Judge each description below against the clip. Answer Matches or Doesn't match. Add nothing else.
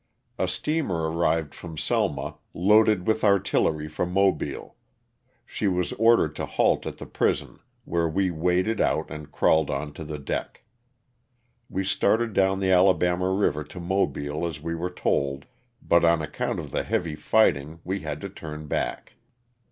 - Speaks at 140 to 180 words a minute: Matches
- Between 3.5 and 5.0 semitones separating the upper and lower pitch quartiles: Matches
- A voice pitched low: Matches